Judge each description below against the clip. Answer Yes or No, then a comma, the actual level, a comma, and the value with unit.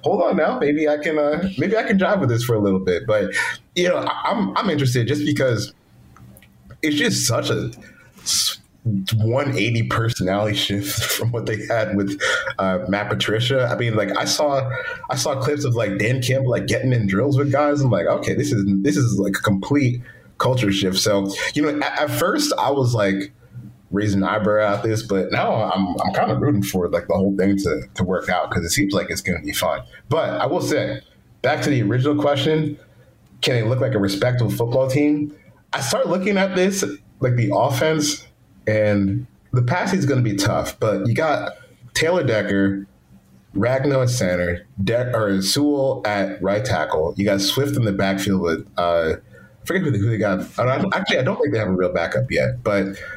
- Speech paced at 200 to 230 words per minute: Yes, fast, 205 wpm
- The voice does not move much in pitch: No, wide, 5.4 semitones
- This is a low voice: Yes, low, 115 Hz